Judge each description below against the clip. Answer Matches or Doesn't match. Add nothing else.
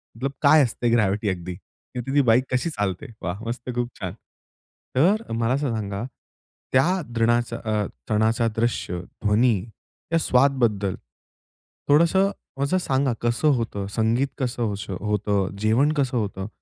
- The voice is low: Matches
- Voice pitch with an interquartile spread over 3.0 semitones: Matches